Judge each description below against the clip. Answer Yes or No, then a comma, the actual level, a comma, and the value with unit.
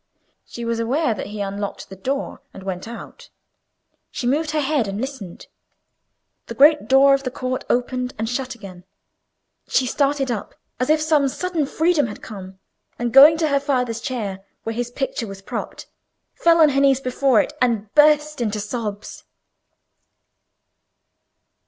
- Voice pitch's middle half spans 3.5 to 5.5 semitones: Yes, average, 4.5 semitones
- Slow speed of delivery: No, average, 160 wpm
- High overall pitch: Yes, very high, 255 Hz